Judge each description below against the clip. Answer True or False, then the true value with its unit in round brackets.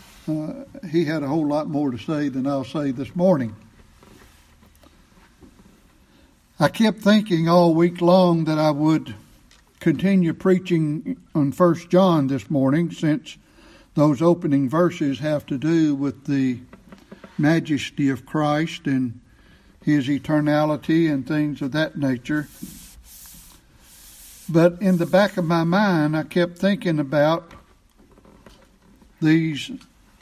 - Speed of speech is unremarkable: False (125 wpm)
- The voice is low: False (155 Hz)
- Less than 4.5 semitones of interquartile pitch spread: True (3.3 semitones)